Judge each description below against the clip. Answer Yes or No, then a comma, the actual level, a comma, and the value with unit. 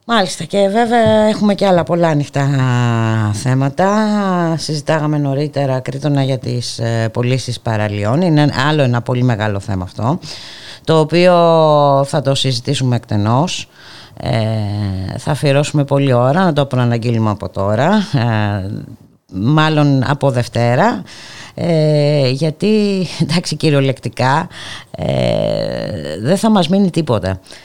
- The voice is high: No, medium, 140 Hz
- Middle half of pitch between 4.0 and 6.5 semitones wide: Yes, average, 5.2 semitones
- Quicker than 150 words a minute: No, slow, 115 wpm